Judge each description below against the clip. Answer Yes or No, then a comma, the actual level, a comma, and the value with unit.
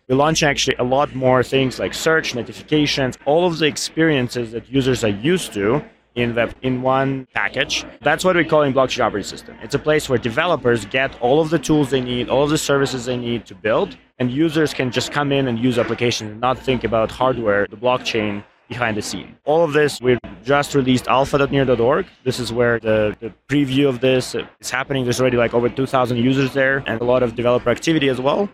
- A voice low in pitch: Yes, low, 130 Hz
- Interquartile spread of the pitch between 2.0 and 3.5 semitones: Yes, average, 2.9 semitones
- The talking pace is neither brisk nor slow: No, fast, 220 wpm